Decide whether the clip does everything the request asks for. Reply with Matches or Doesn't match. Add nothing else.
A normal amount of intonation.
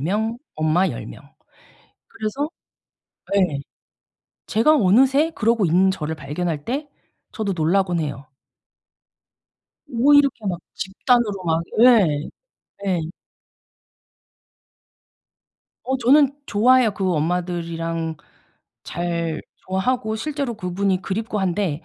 Doesn't match